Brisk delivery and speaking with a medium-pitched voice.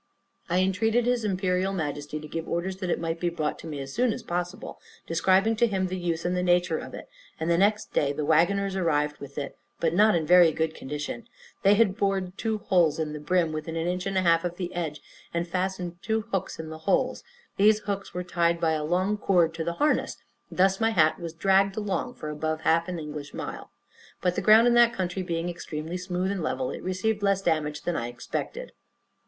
Yes: fast, 225 wpm; medium, 180 Hz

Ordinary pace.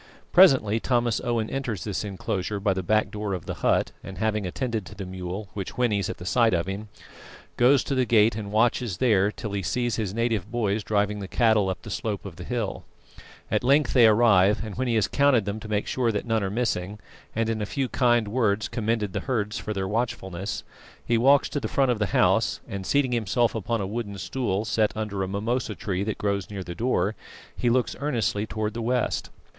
No: fast, 220 wpm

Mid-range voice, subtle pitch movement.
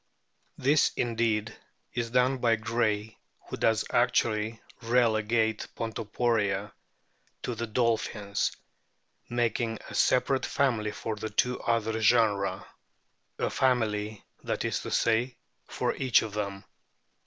No: low, 115 Hz; narrow, 2.1 semitones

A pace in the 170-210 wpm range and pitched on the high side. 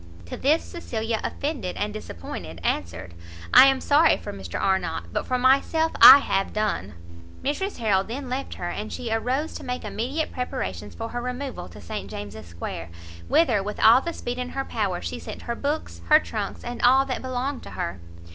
Yes: average, 190 wpm; high, 235 Hz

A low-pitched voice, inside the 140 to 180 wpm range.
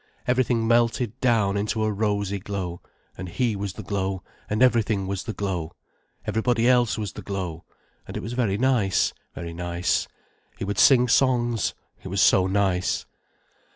Yes: low, 100 Hz; average, 160 wpm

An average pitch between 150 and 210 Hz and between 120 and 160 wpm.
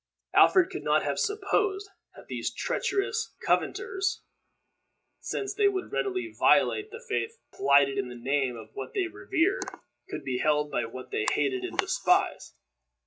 No: very high, 355 Hz; average, 150 wpm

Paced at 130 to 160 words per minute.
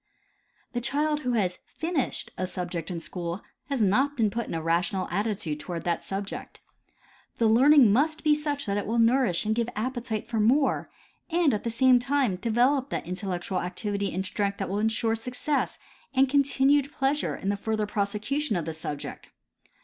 No: average, 180 wpm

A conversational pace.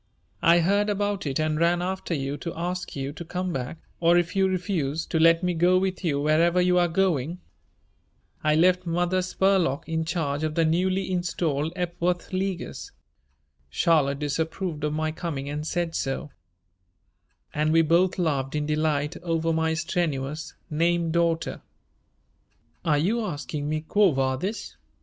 Yes: average, 155 wpm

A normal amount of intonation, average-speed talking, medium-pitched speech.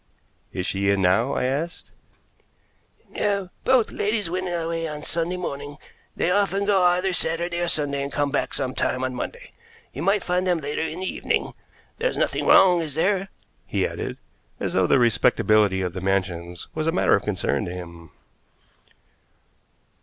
No: wide, 8.9 semitones; average, 170 wpm; medium, 155 Hz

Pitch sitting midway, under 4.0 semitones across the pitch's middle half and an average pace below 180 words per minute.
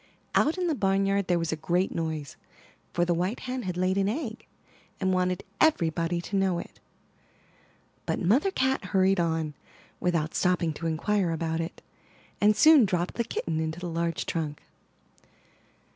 Yes: medium, 180 Hz; average, 3.2 semitones; average, 160 wpm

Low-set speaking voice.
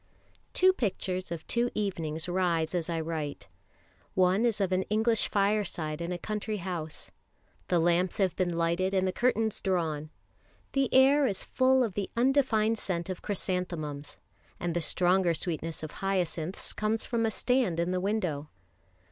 No: medium, 185 Hz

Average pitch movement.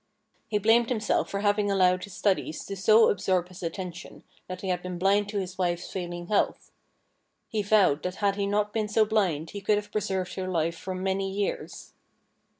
No: narrow, 2.2 semitones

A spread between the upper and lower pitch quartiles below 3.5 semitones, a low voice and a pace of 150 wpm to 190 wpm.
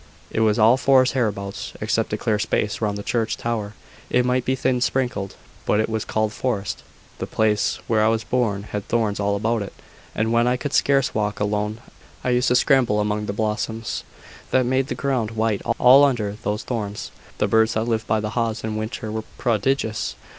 No: average, 2.8 semitones; low, 110 Hz; average, 200 wpm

